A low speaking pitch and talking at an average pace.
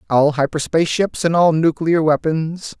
No: medium, 155 Hz; average, 150 wpm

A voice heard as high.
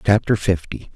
No: low, 100 Hz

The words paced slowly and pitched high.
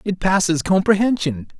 No: slow, 115 wpm; medium, 180 Hz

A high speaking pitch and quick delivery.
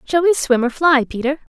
Yes: very high, 285 Hz; fast, 235 wpm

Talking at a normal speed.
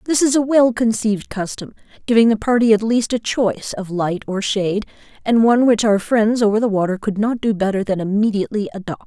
No: fast, 210 wpm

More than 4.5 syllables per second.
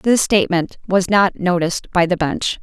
Yes: 4.8 syllables/s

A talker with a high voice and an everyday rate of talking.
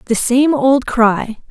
Yes: very high, 250 Hz; average, 160 wpm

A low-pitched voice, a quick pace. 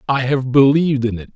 Yes: low, 130 Hz; fast, 220 wpm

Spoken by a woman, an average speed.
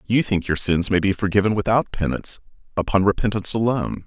No: male; average, 175 wpm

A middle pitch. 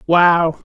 Yes: medium, 170 Hz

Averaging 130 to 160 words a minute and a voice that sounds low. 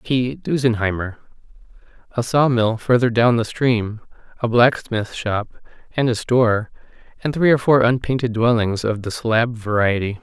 Yes: average, 140 wpm; low, 115 Hz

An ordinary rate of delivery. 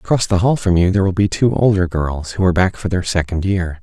No: fast, 280 wpm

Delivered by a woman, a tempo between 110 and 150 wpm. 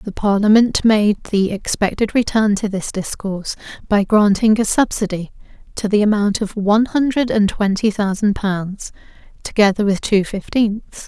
Yes: female; average, 145 wpm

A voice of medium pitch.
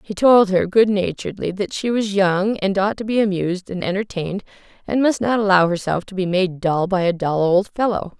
No: high, 195 Hz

